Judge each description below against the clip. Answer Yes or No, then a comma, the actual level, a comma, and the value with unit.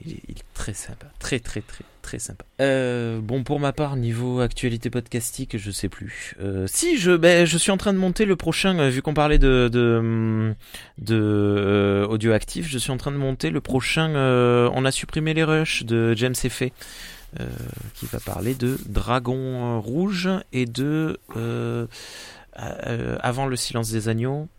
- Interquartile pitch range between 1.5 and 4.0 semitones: No, average, 4.4 semitones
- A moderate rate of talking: Yes, average, 185 wpm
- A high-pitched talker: No, low, 125 Hz